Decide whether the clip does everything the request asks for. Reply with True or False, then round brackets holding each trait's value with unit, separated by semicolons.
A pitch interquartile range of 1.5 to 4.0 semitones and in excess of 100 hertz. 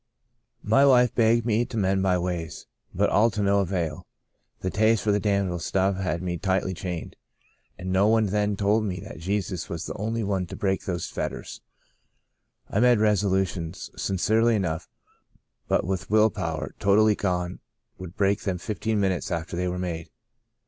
False (2.9 semitones; 95 Hz)